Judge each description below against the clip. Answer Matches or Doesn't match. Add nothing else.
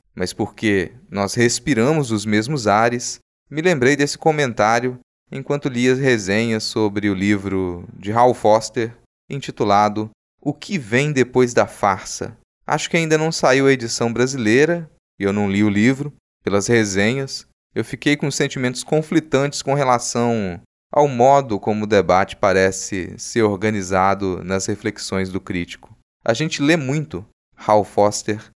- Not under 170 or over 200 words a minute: Doesn't match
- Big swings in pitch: Doesn't match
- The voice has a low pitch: Matches